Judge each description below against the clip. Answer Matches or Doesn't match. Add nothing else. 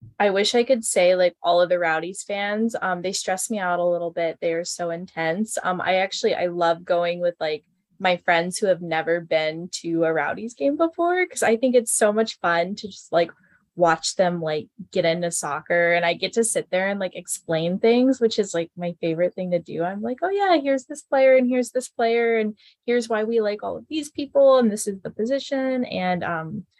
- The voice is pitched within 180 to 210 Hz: Matches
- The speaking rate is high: Matches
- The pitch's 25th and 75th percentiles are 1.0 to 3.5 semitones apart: Doesn't match